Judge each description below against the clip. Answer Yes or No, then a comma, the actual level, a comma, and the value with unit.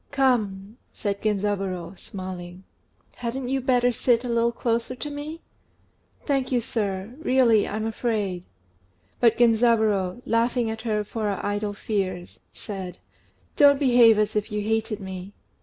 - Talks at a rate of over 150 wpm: No, average, 140 wpm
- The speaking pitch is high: Yes, high, 220 Hz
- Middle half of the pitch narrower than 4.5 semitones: Yes, average, 3.4 semitones